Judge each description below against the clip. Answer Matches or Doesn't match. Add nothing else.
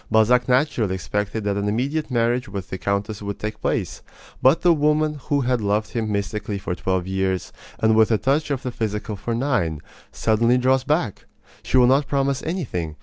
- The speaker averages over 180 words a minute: Matches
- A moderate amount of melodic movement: Matches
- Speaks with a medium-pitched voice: Doesn't match